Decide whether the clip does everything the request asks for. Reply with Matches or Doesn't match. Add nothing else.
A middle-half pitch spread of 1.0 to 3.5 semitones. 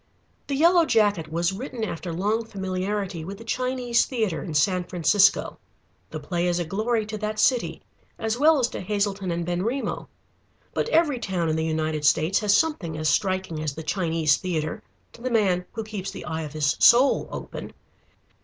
Doesn't match